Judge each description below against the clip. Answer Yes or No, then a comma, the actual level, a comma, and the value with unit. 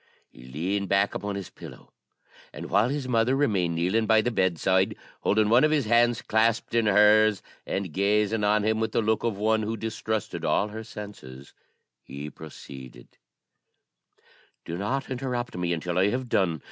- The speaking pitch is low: Yes, low, 105 Hz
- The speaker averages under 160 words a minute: No, average, 170 wpm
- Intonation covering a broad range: No, average, 3.4 semitones